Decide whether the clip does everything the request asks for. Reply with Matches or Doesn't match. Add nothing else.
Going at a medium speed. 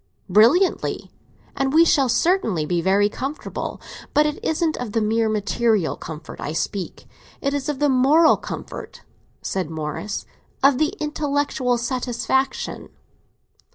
Doesn't match